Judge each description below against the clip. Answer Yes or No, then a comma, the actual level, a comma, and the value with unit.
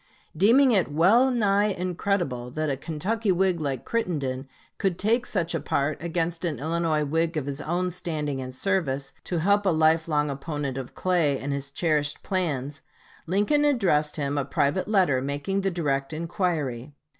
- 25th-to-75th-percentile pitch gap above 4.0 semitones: Yes, average, 4.9 semitones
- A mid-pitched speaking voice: Yes, medium, 160 Hz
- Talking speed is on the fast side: No, average, 165 wpm